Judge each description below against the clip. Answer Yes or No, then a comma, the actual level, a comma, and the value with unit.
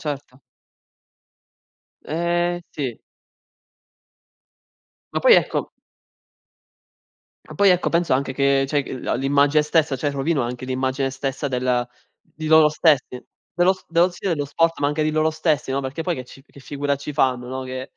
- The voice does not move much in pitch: No, average, 3.3 semitones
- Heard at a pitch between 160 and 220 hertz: No, medium, 145 Hz